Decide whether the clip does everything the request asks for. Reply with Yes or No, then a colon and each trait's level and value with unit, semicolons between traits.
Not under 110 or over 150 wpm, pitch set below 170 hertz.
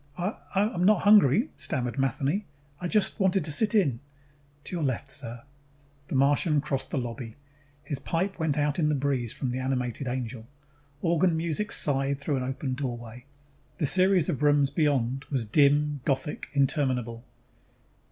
No: average, 160 wpm; medium, 140 Hz